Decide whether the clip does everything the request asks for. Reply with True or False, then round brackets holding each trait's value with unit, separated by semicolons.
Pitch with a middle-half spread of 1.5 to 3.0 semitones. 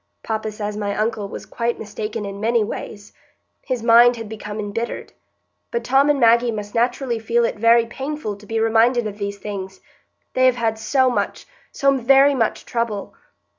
True (2.5 semitones)